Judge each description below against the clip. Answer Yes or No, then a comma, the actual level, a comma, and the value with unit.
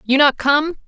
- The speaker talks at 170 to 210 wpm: Yes, fast, 205 wpm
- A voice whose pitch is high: Yes, very high, 285 Hz